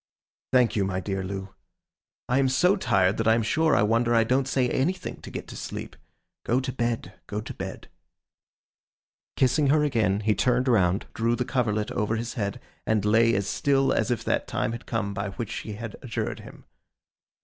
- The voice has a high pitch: No, low, 115 Hz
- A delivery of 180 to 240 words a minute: Yes, average, 195 wpm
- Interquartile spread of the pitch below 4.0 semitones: Yes, average, 3.5 semitones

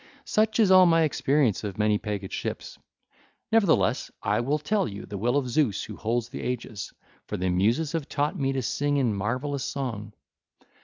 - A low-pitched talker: Yes, low, 130 Hz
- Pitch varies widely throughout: Yes, wide, 6.1 semitones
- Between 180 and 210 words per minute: Yes, average, 185 wpm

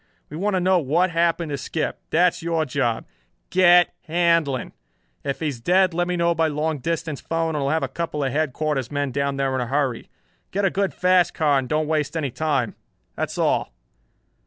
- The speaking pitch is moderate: Yes, medium, 155 Hz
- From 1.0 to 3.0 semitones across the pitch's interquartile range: No, average, 3.4 semitones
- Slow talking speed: No, fast, 205 wpm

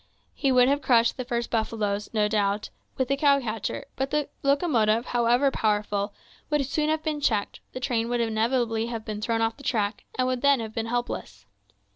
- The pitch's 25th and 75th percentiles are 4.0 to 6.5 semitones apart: No, average, 3.6 semitones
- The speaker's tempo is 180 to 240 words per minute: Yes, average, 195 wpm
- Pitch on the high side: Yes, high, 235 Hz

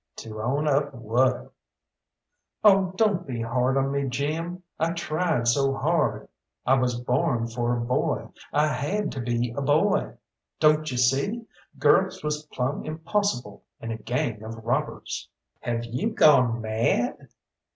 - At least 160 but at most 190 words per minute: No, average, 145 wpm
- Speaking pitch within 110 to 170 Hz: Yes, low, 135 Hz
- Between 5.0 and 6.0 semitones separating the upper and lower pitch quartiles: No, average, 4.6 semitones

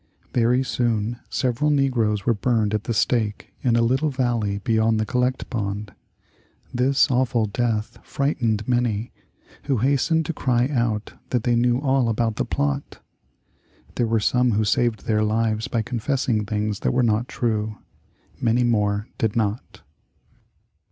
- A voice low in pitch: Yes, low, 115 Hz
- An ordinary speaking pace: Yes, average, 150 wpm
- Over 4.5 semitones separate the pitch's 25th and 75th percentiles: No, average, 2.7 semitones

